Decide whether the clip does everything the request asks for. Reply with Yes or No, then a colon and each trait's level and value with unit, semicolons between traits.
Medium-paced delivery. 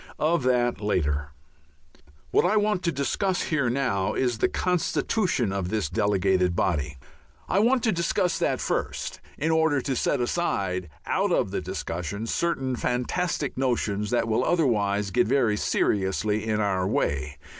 Yes: average, 150 wpm